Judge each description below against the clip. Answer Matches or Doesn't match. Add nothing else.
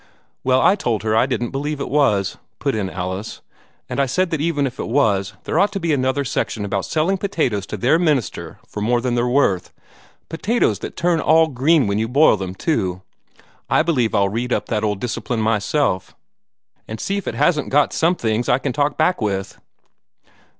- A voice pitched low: Matches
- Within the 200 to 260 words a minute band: Matches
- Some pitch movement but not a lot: Doesn't match